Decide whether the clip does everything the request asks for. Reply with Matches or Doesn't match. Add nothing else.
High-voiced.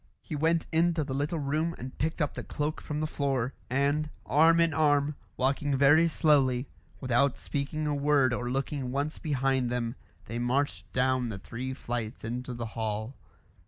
Doesn't match